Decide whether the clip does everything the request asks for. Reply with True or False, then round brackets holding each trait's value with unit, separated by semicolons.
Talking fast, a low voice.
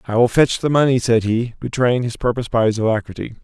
True (225 wpm; 120 Hz)